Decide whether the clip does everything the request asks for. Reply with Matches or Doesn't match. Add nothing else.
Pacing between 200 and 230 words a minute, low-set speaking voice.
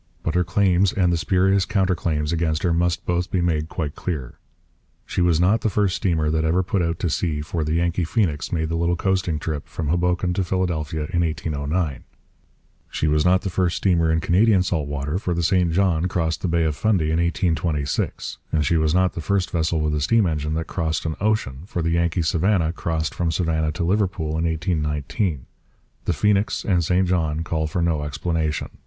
Matches